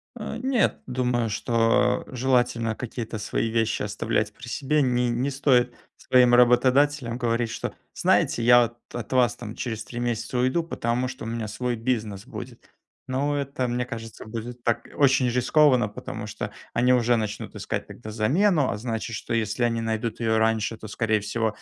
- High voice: No, low, 120 Hz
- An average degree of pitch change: No, narrow, 2.2 semitones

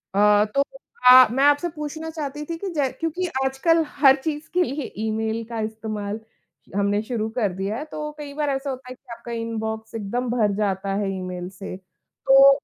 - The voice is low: No, very high, 250 Hz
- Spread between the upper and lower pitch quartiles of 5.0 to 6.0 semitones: Yes, wide, 5.4 semitones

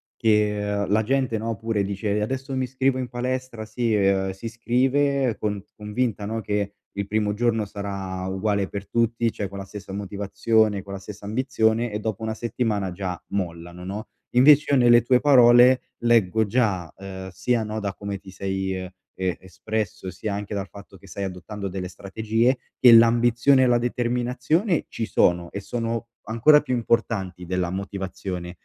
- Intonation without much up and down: No, average, 3.5 semitones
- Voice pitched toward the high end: No, low, 105 Hz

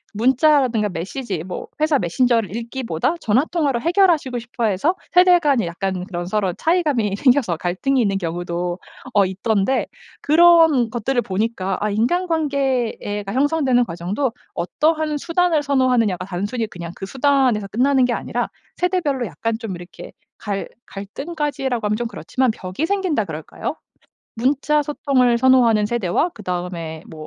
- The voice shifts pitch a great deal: Yes, wide, 6.5 semitones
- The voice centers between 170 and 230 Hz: No, high, 240 Hz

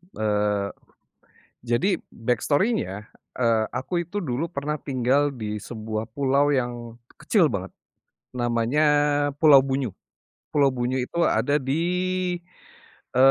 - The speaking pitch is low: Yes, low, 130 Hz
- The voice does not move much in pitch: No, average, 3.8 semitones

